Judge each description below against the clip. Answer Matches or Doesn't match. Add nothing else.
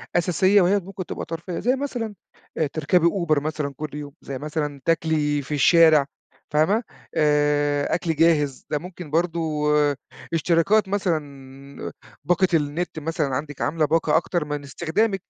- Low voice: Doesn't match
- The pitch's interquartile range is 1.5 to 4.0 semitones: Matches